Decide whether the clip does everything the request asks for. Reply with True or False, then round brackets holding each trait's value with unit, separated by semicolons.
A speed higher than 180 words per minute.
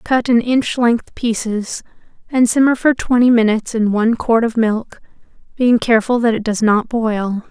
False (175 wpm)